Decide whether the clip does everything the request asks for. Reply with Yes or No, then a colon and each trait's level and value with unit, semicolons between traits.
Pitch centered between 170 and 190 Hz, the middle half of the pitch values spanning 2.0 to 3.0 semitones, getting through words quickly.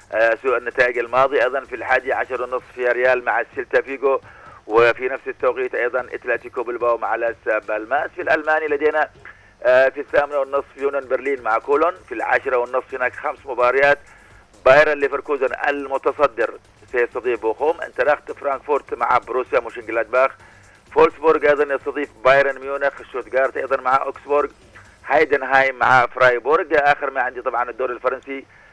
No: low, 135 Hz; average, 2.7 semitones; fast, 140 wpm